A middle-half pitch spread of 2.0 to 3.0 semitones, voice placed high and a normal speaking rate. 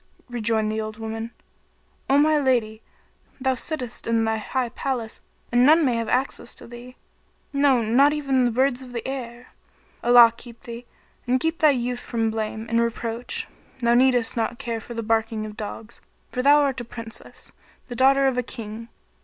Yes: narrow, 2.5 semitones; high, 240 Hz; average, 180 wpm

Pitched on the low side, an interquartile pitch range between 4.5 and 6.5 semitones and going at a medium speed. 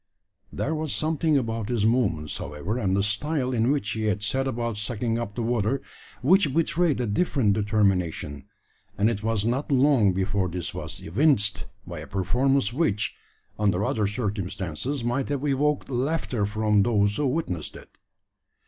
Yes: low, 115 Hz; average, 5.0 semitones; average, 160 wpm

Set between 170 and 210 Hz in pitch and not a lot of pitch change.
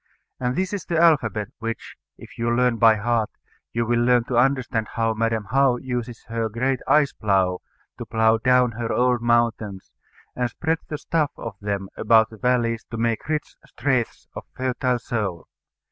No: low, 120 Hz; narrow, 2.2 semitones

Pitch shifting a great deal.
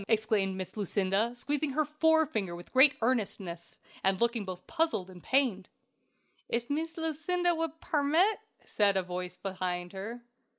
Yes: wide, 8.0 semitones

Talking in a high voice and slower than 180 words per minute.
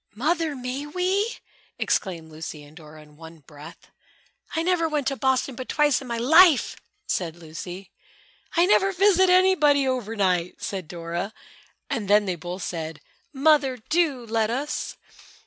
Yes: high, 245 Hz; average, 150 wpm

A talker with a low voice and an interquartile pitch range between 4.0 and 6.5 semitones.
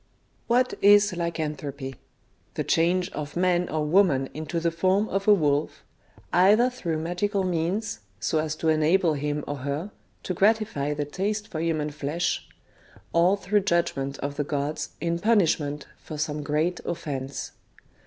No: medium, 165 Hz; average, 4.3 semitones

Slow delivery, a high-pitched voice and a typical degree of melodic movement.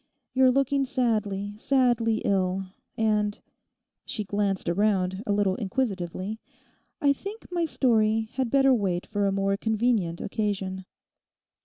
Yes: slow, 125 wpm; high, 210 Hz; average, 4.2 semitones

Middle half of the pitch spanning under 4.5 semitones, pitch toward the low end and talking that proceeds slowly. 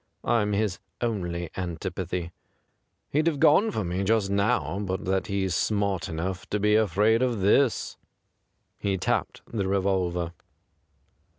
Yes: average, 2.9 semitones; low, 100 Hz; slow, 130 wpm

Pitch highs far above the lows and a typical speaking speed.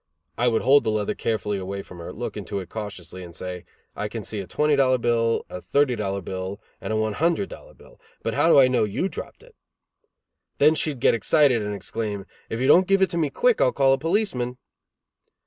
No: wide, 6.2 semitones; fast, 225 wpm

